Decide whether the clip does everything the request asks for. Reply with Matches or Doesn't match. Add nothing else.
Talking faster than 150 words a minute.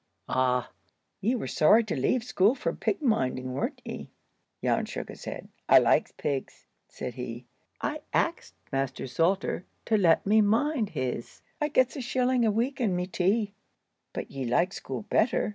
Matches